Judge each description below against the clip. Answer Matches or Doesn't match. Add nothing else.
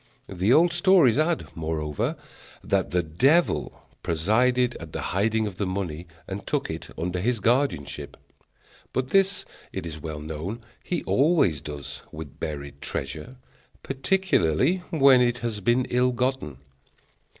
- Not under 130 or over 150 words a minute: Matches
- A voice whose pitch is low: Matches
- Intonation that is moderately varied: Doesn't match